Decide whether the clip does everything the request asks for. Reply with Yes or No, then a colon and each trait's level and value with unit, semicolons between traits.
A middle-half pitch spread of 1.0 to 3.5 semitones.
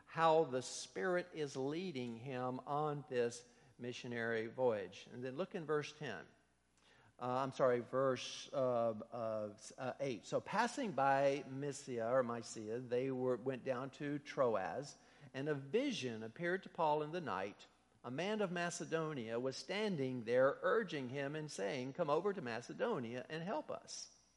No: average, 4.2 semitones